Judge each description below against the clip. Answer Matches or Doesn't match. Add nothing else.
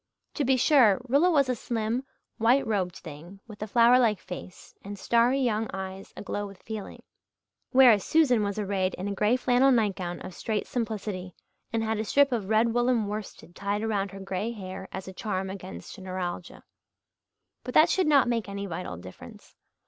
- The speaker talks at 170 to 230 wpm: Matches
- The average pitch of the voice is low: Doesn't match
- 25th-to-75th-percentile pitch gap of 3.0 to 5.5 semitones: Matches